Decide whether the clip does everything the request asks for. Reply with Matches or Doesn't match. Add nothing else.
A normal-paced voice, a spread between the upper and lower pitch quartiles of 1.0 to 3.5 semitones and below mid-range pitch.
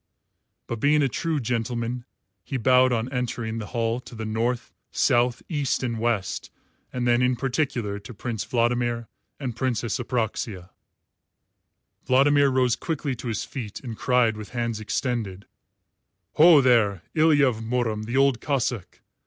Matches